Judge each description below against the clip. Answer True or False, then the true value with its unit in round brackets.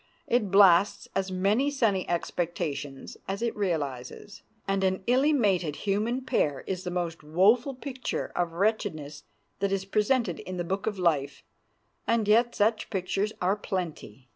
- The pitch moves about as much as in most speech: True (4.0 semitones)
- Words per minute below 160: True (150 wpm)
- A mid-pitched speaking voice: False (195 Hz)